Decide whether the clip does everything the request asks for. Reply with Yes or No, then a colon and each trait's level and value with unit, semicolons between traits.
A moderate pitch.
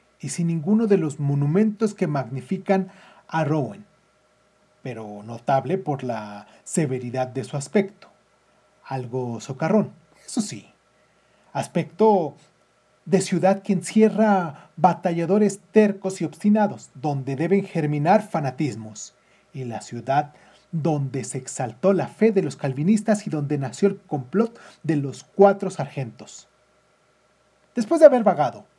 Yes: medium, 165 Hz